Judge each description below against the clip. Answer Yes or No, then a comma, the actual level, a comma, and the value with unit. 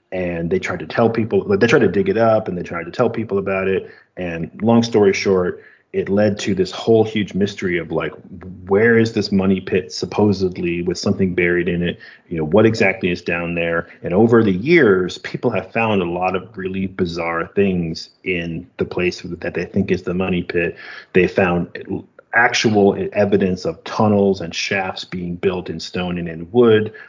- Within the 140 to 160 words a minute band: No, average, 195 wpm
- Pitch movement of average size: Yes, average, 4.1 semitones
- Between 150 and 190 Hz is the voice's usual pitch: No, very low, 95 Hz